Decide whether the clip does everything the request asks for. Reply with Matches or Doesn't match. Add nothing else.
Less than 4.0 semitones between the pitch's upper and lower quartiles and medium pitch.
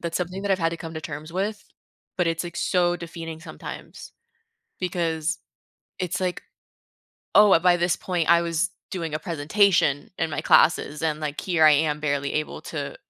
Matches